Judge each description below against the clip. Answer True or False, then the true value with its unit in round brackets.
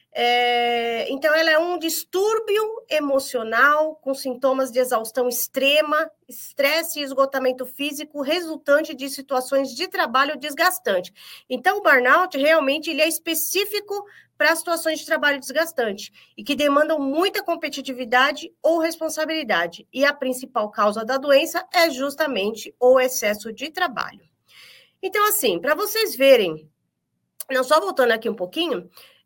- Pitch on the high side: True (290 Hz)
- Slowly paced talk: False (130 wpm)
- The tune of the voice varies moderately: True (4.0 semitones)